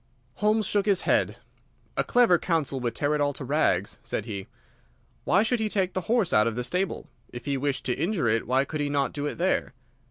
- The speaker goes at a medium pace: No, fast, 225 wpm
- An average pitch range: No, wide, 6.8 semitones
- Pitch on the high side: No, medium, 150 Hz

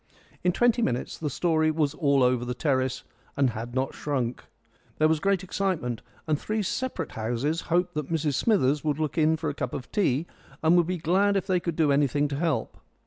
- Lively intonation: No, average, 4.6 semitones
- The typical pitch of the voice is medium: Yes, medium, 155 Hz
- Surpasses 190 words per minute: Yes, fast, 205 wpm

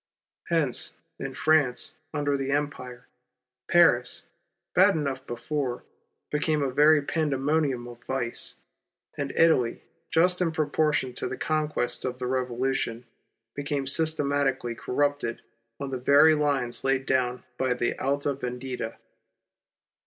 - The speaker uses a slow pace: Yes, slow, 125 wpm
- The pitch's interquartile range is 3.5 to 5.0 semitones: No, average, 2.9 semitones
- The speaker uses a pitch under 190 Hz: Yes, low, 135 Hz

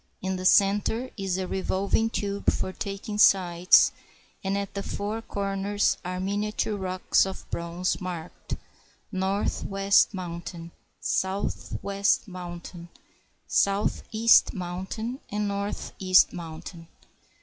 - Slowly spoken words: Yes, slow, 105 wpm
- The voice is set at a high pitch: Yes, high, 195 Hz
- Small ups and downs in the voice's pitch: Yes, narrow, 1.7 semitones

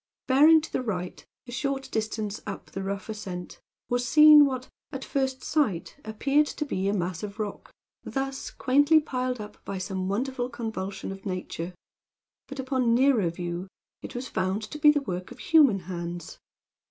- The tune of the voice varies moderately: No, wide, 5.9 semitones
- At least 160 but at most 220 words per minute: Yes, average, 170 wpm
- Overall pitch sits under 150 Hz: No, high, 225 Hz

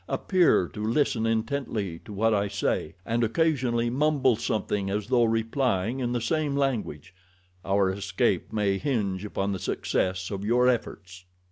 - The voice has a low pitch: Yes, low, 110 Hz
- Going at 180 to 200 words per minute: No, average, 145 wpm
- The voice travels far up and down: No, average, 4.2 semitones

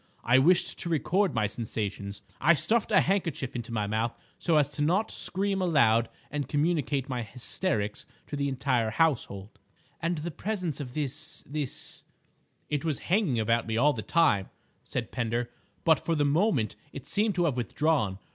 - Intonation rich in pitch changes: Yes, wide, 6.2 semitones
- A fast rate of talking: No, average, 165 wpm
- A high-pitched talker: No, medium, 145 Hz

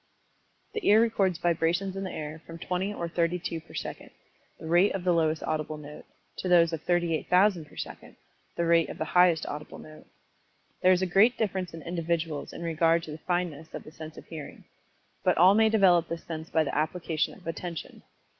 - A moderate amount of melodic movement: No, narrow, 2.3 semitones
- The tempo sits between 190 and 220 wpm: Yes, average, 200 wpm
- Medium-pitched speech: Yes, medium, 170 Hz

